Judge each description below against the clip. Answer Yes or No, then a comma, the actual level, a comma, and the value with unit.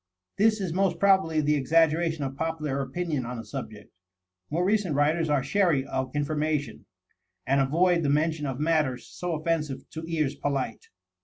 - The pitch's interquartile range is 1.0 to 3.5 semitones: Yes, average, 3.2 semitones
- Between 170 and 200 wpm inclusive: No, average, 160 wpm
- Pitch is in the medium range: Yes, medium, 155 Hz